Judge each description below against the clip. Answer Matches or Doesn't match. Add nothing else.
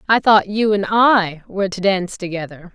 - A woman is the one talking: Matches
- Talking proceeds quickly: Doesn't match